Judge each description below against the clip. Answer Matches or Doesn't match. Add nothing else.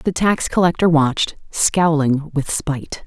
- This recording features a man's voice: Doesn't match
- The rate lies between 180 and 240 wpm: Doesn't match